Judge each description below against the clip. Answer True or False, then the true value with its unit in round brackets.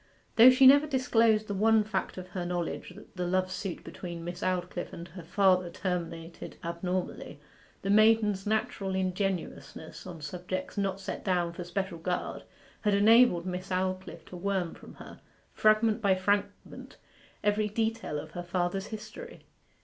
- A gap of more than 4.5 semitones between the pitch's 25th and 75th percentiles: False (3.1 semitones)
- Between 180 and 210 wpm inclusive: False (155 wpm)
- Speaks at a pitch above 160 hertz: True (190 Hz)